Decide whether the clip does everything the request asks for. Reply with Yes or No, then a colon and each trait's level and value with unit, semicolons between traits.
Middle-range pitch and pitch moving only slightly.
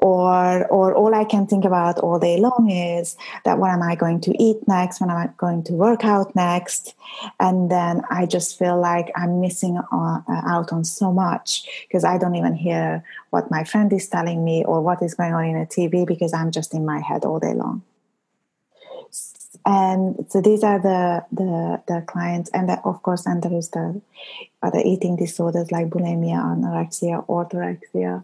Yes: medium, 175 Hz; narrow, 1.8 semitones